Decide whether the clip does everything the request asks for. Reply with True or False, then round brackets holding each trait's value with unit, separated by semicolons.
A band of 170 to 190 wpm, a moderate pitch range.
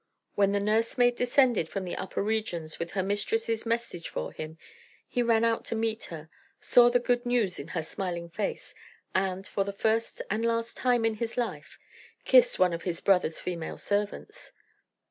True (180 wpm; 4.4 semitones)